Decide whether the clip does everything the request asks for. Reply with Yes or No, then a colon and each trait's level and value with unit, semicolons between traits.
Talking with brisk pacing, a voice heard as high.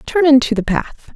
Yes: fast, 210 wpm; very high, 270 Hz